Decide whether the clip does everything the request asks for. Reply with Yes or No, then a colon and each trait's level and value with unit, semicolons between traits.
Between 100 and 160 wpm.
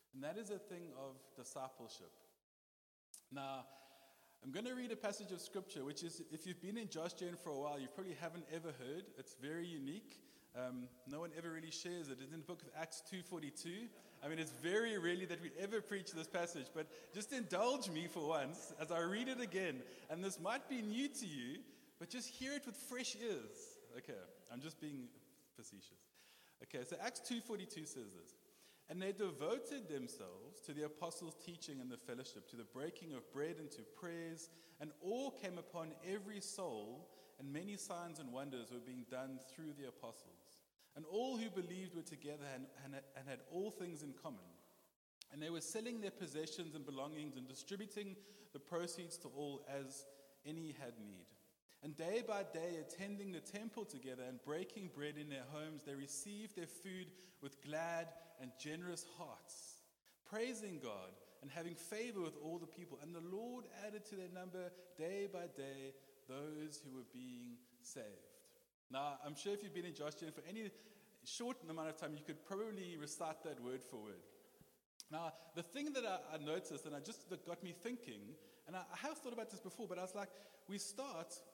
No: average, 190 wpm